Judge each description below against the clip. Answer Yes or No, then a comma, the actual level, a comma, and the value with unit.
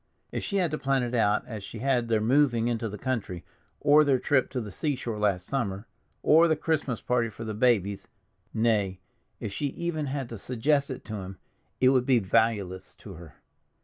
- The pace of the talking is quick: No, average, 195 wpm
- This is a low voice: Yes, low, 120 Hz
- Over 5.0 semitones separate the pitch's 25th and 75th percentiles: No, average, 4.6 semitones